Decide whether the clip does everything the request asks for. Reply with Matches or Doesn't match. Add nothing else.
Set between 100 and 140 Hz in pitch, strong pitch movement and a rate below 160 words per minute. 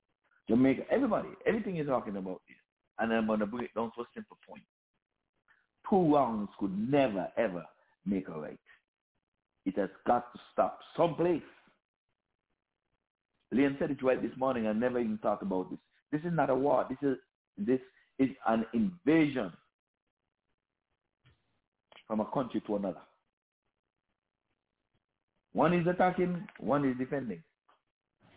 Matches